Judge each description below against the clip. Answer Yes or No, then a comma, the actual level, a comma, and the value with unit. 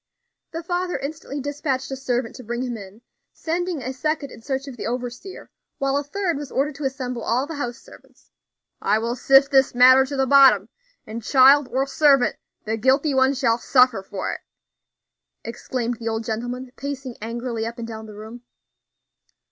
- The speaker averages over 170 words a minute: Yes, average, 180 wpm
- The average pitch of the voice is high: Yes, very high, 260 Hz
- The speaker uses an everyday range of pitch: Yes, average, 3.0 semitones